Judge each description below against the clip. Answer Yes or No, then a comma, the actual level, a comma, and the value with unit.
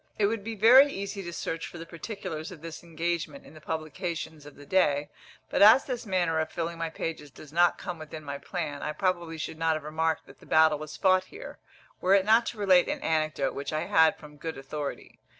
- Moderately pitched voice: Yes, medium, 165 Hz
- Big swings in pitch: No, average, 3.4 semitones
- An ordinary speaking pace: No, fast, 225 wpm